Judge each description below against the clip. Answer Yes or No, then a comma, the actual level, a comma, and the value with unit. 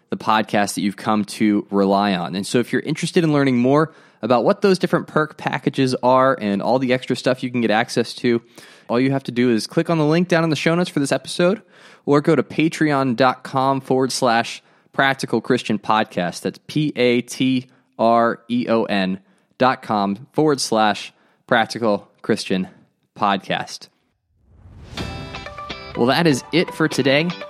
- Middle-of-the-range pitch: No, low, 130 Hz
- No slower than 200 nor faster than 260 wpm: No, average, 165 wpm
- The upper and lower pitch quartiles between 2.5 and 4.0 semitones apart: No, average, 5.1 semitones